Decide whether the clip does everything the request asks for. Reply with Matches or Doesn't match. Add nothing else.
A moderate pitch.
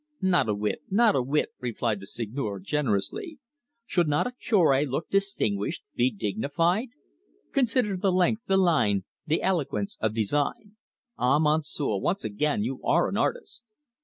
Matches